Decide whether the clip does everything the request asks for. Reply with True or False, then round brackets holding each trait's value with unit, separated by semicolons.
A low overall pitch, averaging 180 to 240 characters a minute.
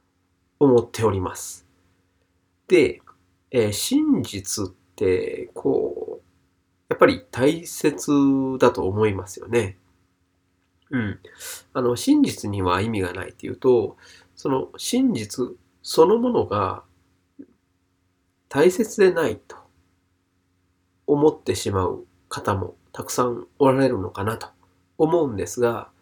True (110 Hz; 200 characters per minute)